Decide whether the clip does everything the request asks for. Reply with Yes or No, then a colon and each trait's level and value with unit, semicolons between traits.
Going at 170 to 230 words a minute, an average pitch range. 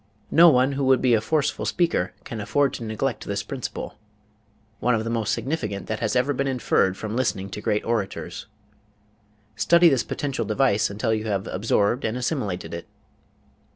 Yes: average, 175 wpm; average, 4.4 semitones